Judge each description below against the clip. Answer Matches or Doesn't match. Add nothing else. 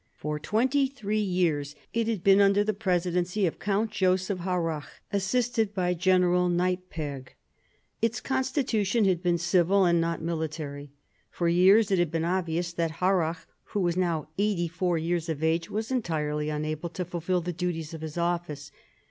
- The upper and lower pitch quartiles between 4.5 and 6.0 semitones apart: Doesn't match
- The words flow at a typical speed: Matches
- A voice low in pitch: Doesn't match